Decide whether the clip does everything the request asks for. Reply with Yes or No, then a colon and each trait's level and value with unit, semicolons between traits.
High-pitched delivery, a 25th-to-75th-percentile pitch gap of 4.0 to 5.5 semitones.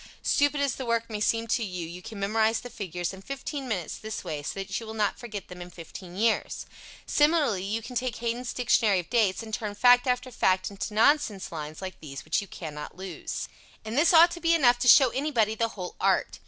Yes: high, 220 Hz; average, 4.8 semitones